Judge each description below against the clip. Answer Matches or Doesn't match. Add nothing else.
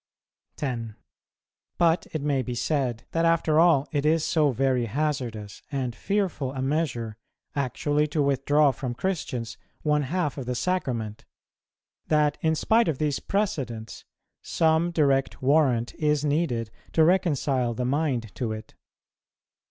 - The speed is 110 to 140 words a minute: Matches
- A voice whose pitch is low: Doesn't match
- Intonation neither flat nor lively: Matches